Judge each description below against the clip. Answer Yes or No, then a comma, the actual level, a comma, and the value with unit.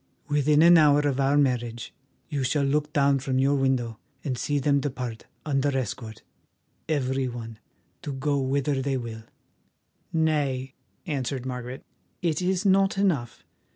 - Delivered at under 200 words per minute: Yes, average, 145 wpm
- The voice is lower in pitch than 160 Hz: Yes, low, 135 Hz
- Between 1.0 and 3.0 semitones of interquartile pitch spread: Yes, narrow, 2.5 semitones